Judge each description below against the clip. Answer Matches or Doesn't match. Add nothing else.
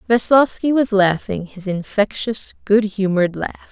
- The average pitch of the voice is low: Doesn't match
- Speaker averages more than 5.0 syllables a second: Doesn't match